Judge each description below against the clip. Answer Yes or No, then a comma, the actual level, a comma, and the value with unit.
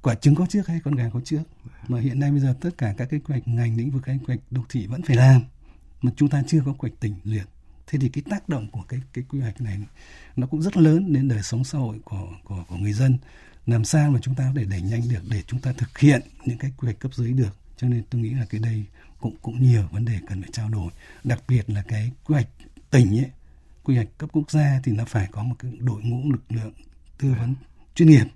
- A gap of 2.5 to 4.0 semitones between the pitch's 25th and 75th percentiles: Yes, average, 3.6 semitones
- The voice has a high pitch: No, low, 125 Hz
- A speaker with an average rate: No, fast, 275 wpm